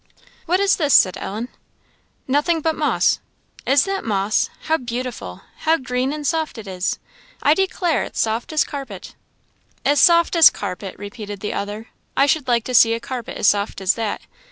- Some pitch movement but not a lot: No, wide, 6.7 semitones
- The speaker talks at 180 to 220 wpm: Yes, average, 190 wpm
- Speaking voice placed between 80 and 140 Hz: No, very high, 250 Hz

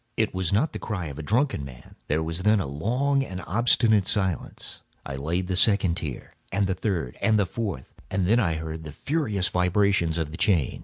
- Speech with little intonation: No, average, 4.9 semitones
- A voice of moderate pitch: No, very low, 95 Hz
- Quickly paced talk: Yes, fast, 210 wpm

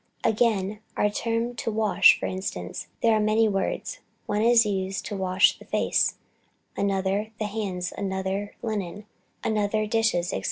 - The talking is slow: No, average, 160 wpm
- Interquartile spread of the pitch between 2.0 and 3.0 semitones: Yes, narrow, 2.4 semitones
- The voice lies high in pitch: Yes, high, 205 Hz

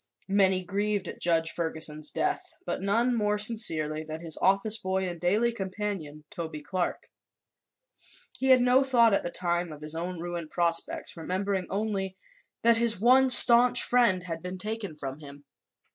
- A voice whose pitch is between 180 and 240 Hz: Yes, high, 190 Hz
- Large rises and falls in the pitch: No, average, 4.9 semitones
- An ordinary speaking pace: Yes, average, 160 wpm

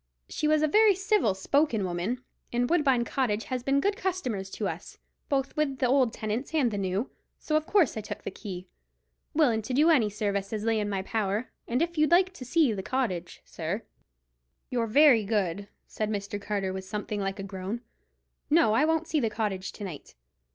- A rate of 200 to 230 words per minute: Yes, fast, 205 wpm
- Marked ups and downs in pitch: Yes, wide, 6.6 semitones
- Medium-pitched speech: No, high, 230 Hz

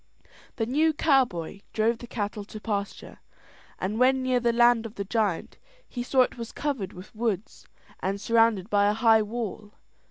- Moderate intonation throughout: Yes, average, 3.0 semitones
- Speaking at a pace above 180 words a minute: No, average, 170 wpm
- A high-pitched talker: Yes, high, 225 Hz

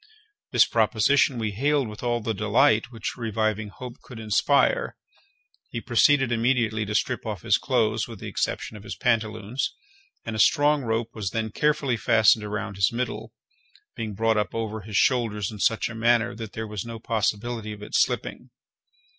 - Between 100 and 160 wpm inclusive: No, average, 175 wpm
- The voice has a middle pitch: No, low, 110 Hz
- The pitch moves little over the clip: Yes, narrow, 1.9 semitones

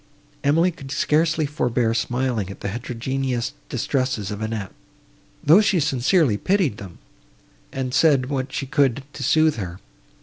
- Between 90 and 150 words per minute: Yes, average, 140 wpm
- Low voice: Yes, low, 130 Hz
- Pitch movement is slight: No, average, 4.5 semitones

